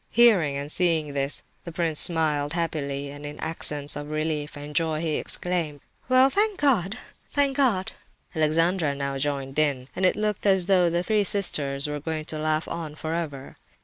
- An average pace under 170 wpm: No, average, 175 wpm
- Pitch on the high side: No, medium, 155 Hz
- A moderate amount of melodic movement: Yes, average, 3.7 semitones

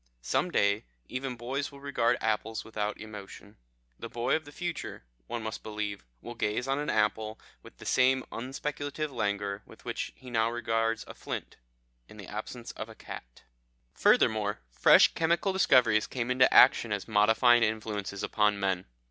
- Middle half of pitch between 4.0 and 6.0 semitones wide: No, average, 3.5 semitones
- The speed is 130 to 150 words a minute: No, average, 165 wpm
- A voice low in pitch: Yes, low, 115 Hz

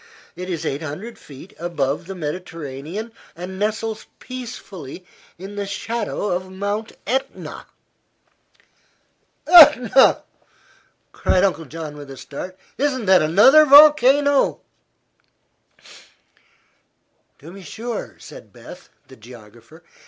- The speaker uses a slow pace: Yes, slow, 105 wpm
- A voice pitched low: No, high, 190 Hz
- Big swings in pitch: Yes, wide, 6.8 semitones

